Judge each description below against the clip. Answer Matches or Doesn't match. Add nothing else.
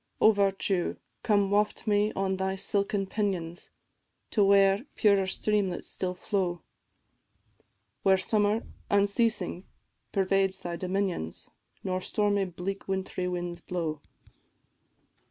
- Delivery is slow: Matches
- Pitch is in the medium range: Doesn't match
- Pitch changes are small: Matches